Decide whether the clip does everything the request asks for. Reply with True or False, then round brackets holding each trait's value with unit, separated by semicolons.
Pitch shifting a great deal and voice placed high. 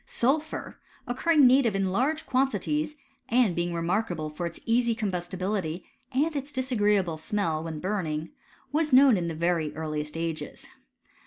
True (7.6 semitones; 200 Hz)